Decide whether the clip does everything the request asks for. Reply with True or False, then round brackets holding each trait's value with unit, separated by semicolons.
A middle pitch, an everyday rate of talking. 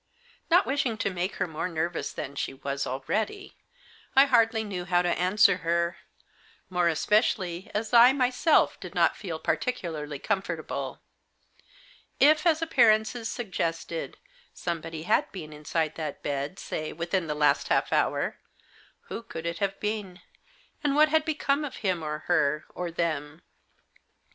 True (180 Hz; 150 wpm)